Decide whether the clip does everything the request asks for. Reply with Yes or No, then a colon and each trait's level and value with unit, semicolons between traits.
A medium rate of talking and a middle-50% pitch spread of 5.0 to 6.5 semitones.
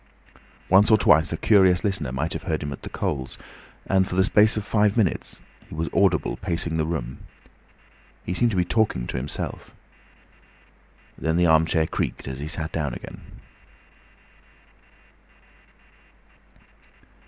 No: average, 145 wpm; average, 4.0 semitones